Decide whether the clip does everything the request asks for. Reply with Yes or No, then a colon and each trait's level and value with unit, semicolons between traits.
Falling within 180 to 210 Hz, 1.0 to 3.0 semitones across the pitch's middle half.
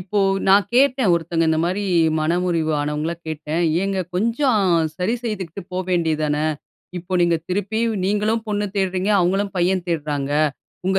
No: medium, 185 Hz; average, 3.7 semitones